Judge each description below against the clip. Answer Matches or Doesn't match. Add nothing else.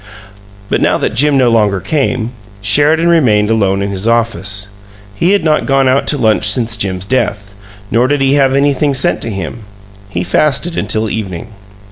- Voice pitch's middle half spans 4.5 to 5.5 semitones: Matches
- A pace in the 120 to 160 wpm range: Doesn't match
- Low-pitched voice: Matches